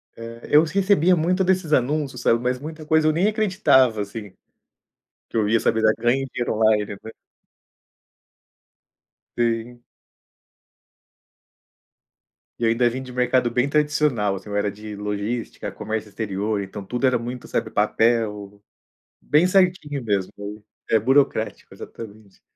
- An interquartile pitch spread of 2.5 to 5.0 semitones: No, wide, 5.6 semitones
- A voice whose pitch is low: Yes, low, 120 Hz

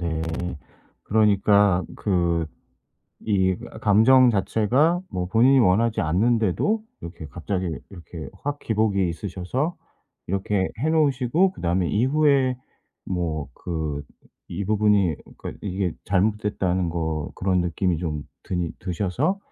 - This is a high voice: No, low, 100 Hz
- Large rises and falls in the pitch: No, average, 4.9 semitones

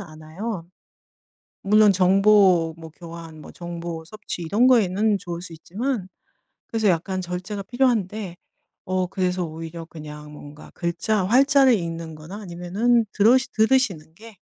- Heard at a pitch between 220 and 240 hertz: No, medium, 185 Hz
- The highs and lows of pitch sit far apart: No, average, 4.3 semitones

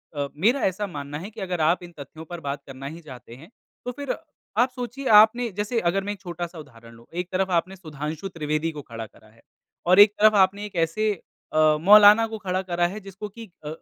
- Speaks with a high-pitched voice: No, medium, 180 Hz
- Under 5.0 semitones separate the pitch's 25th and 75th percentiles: No, average, 5.3 semitones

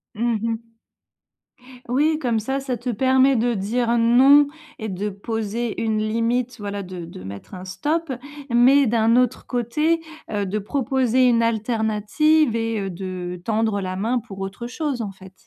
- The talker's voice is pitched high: Yes, high, 230 Hz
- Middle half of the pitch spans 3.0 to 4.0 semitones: Yes, average, 3.6 semitones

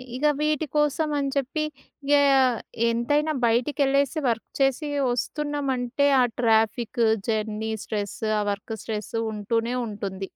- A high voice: Yes, high, 245 Hz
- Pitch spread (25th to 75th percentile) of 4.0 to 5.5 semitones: Yes, average, 4.5 semitones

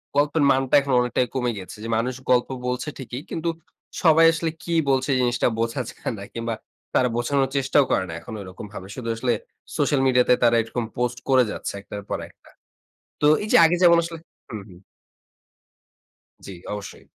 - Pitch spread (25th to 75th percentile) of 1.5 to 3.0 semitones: No, average, 3.4 semitones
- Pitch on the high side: No, low, 125 Hz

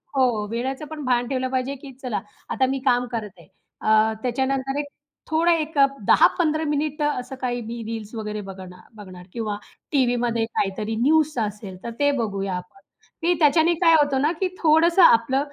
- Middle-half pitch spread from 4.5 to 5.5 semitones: Yes, average, 5.1 semitones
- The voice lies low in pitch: No, very high, 255 Hz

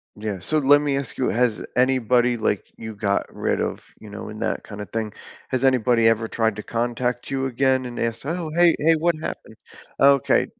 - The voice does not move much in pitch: No, average, 3.4 semitones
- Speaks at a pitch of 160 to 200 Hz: No, low, 120 Hz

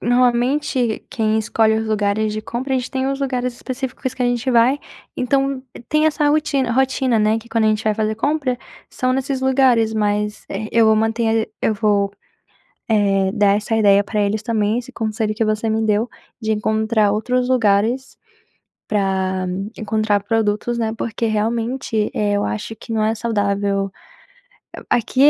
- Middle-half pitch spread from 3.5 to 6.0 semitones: No, average, 2.9 semitones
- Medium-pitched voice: No, high, 225 Hz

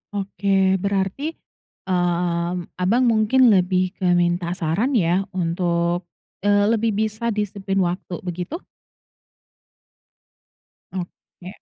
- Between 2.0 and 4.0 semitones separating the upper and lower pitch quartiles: Yes, average, 2.7 semitones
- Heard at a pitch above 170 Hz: Yes, medium, 185 Hz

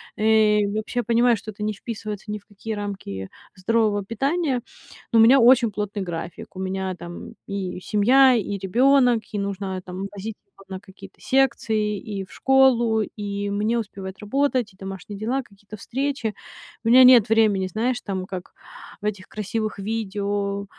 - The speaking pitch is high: Yes, high, 210 Hz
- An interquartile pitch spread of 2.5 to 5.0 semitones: Yes, average, 2.8 semitones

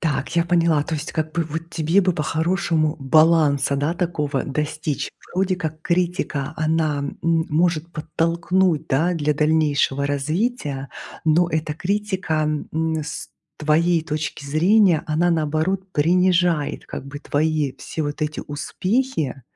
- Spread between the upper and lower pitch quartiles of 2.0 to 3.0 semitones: Yes, narrow, 2.4 semitones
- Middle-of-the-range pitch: Yes, medium, 160 Hz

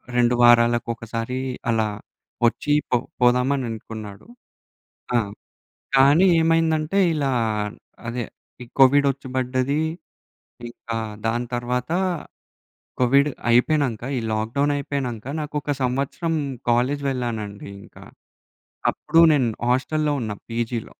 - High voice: No, low, 125 Hz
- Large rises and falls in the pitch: No, average, 3.3 semitones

